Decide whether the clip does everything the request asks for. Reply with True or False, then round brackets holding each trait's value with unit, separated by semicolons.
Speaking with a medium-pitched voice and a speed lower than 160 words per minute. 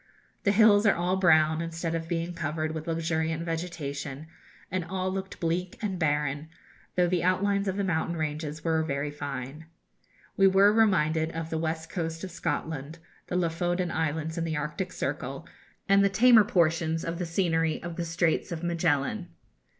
False (165 Hz; 170 wpm)